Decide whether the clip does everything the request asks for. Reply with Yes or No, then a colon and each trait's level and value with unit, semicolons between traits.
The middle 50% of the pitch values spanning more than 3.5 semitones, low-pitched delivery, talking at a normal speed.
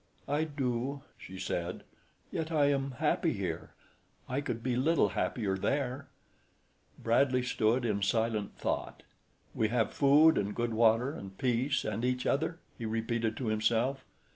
Yes: average, 4.1 semitones; low, 120 Hz; average, 145 wpm